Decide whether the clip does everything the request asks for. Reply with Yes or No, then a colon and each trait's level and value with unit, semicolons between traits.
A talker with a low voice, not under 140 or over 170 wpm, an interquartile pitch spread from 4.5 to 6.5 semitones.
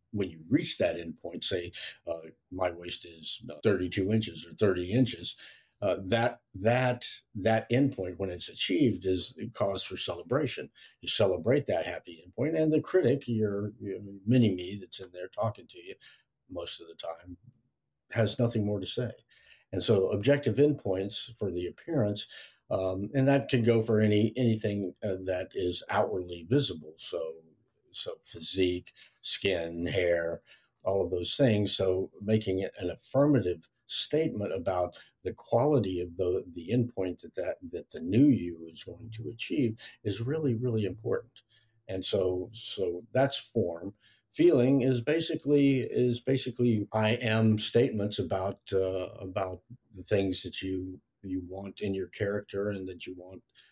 Yes: low, 105 Hz; average, 155 wpm; average, 4.9 semitones